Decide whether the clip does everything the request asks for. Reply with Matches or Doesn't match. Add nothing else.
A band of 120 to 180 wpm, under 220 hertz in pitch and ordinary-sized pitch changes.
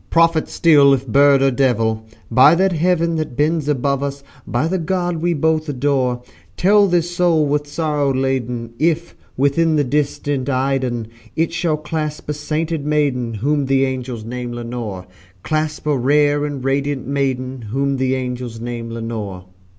Matches